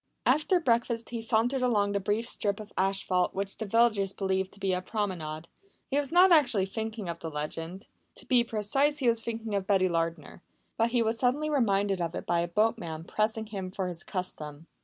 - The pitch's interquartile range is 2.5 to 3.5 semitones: No, average, 4.1 semitones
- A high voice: Yes, high, 205 Hz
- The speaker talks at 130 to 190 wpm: No, average, 200 wpm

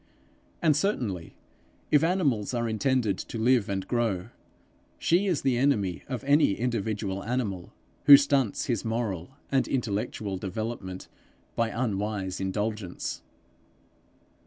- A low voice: Yes, low, 115 Hz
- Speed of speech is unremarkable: No, slow, 115 wpm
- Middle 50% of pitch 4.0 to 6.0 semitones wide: Yes, average, 5.0 semitones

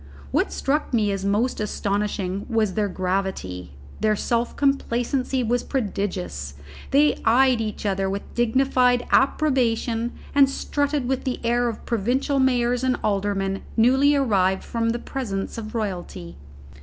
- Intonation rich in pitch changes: No, average, 4.5 semitones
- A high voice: Yes, high, 230 Hz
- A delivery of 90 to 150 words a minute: Yes, slow, 135 wpm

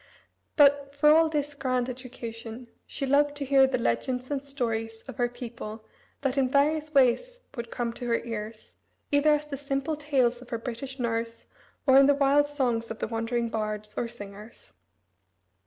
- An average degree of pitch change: Yes, average, 3.6 semitones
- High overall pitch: Yes, very high, 255 Hz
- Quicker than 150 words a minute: Yes, average, 175 wpm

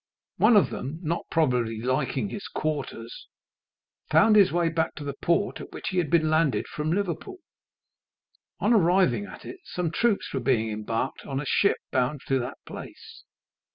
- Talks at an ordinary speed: Yes, average, 170 wpm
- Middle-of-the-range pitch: Yes, medium, 155 Hz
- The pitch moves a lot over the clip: Yes, wide, 5.7 semitones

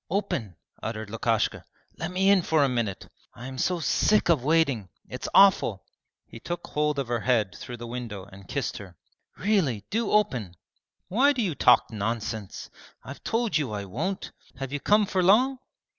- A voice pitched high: No, low, 135 Hz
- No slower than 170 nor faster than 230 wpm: Yes, average, 175 wpm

